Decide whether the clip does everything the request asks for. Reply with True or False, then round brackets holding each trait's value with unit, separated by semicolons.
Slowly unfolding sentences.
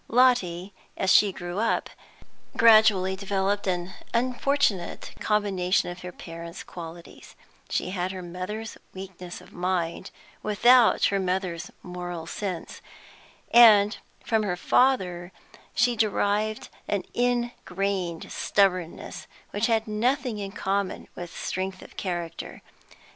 True (115 wpm)